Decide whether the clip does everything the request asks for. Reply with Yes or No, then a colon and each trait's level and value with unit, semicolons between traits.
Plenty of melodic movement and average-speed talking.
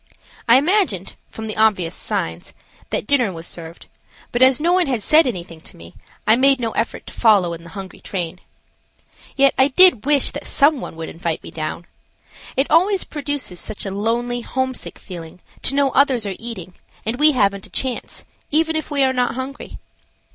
Yes: wide, 6.9 semitones; average, 190 wpm